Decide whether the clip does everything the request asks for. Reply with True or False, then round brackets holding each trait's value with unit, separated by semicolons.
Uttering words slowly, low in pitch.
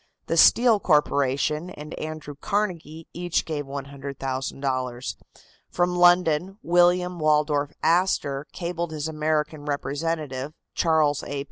False (105 wpm; 155 Hz)